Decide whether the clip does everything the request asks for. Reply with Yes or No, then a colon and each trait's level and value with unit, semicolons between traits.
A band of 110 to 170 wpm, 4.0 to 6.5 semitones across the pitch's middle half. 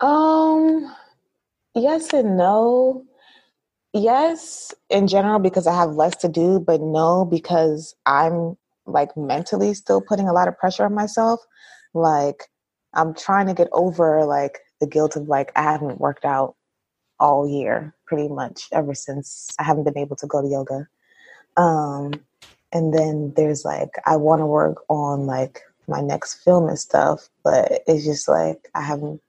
Yes: average, 160 wpm; average, 5.1 semitones